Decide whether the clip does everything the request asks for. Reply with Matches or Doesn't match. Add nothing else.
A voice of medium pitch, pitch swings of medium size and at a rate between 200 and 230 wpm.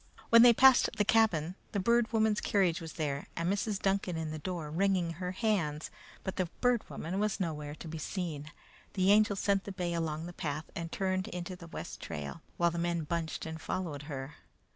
Matches